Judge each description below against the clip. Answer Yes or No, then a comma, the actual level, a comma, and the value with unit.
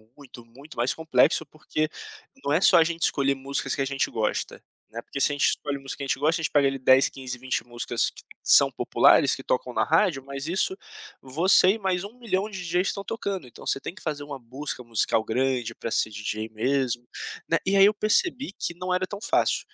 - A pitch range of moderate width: No, wide, 5.8 semitones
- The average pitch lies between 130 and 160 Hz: Yes, medium, 140 Hz